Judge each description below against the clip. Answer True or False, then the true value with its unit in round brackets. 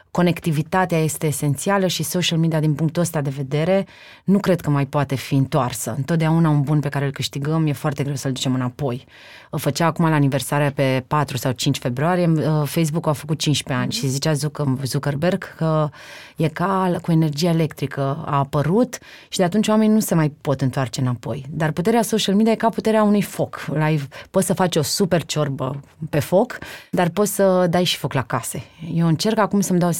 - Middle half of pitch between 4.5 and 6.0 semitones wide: False (3.9 semitones)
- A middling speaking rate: False (195 wpm)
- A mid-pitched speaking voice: True (155 Hz)